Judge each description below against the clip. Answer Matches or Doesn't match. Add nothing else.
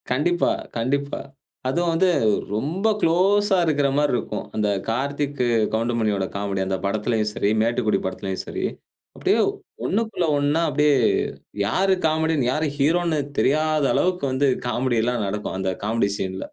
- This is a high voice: Doesn't match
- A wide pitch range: Matches